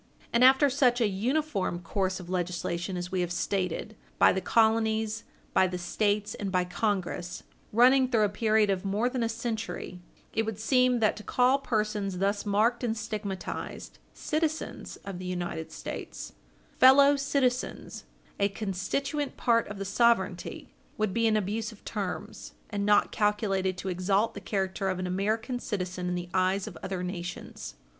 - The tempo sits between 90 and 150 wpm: No, average, 165 wpm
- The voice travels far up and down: No, average, 3.7 semitones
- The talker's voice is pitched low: No, high, 205 Hz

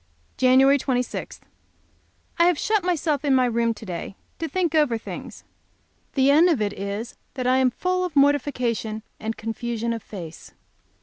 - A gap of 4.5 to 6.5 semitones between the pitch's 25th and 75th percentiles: Yes, average, 4.8 semitones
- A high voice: Yes, very high, 255 Hz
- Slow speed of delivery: No, average, 170 wpm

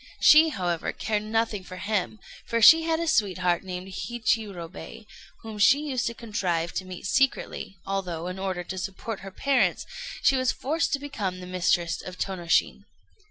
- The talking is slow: No, average, 165 wpm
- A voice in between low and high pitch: No, high, 195 Hz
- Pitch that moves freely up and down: No, average, 4.7 semitones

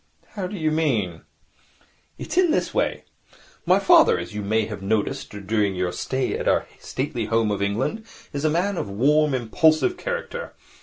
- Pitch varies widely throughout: Yes, wide, 8.8 semitones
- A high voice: No, low, 130 Hz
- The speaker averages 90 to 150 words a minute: No, average, 175 wpm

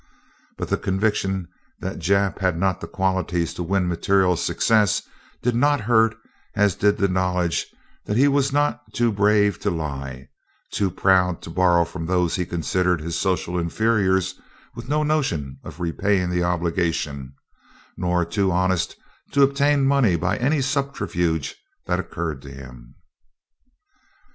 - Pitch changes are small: No, average, 3.9 semitones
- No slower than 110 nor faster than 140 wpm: No, average, 150 wpm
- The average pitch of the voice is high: No, very low, 95 Hz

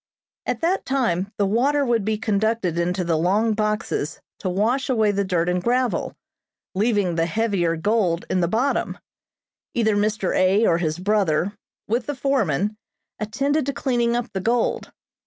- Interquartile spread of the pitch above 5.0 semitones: No, average, 4.5 semitones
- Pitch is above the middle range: Yes, high, 210 Hz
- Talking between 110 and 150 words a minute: No, average, 160 wpm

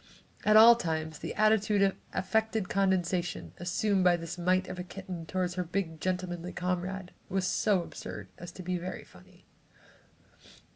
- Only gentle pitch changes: Yes, narrow, 1.9 semitones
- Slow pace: No, average, 155 wpm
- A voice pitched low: No, medium, 185 Hz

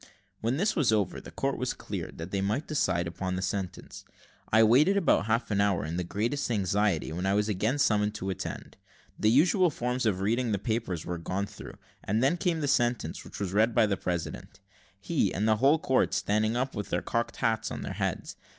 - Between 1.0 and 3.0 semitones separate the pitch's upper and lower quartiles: No, average, 4.3 semitones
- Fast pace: Yes, fast, 215 wpm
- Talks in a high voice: No, low, 110 Hz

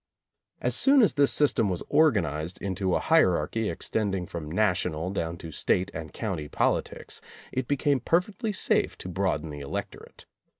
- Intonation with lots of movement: Yes, wide, 8.8 semitones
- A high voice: No, very low, 95 Hz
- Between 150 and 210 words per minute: Yes, average, 155 wpm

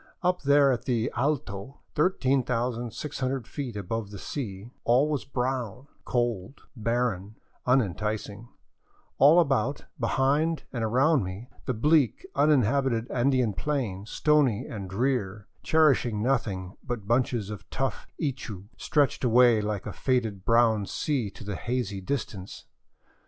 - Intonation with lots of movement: No, average, 4.3 semitones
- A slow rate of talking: Yes, slow, 130 wpm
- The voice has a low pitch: Yes, low, 120 Hz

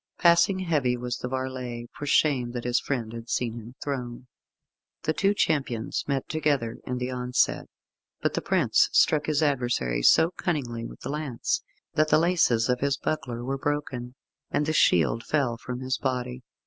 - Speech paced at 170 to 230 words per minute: Yes, average, 175 wpm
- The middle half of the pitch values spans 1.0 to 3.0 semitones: No, average, 3.5 semitones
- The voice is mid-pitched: No, low, 130 Hz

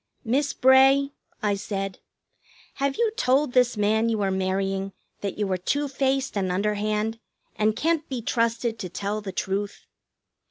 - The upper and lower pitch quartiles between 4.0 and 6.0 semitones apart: Yes, average, 5.0 semitones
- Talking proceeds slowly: No, average, 155 wpm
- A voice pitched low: No, high, 215 Hz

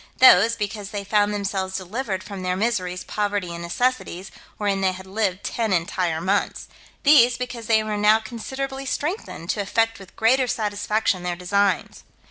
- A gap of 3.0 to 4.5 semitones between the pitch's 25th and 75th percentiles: Yes, average, 3.3 semitones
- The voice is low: No, high, 205 Hz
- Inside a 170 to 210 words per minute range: No, average, 160 wpm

